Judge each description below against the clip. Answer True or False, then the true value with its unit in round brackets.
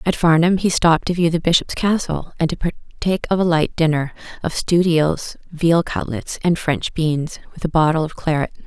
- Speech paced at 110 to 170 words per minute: False (200 wpm)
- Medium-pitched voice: True (165 Hz)